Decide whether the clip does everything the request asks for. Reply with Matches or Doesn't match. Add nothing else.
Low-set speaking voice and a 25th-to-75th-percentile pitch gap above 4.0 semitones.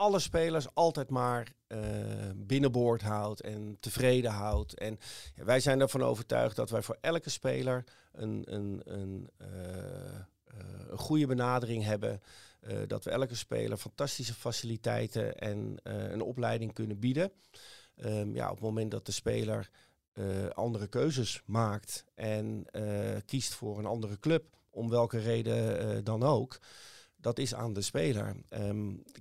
Doesn't match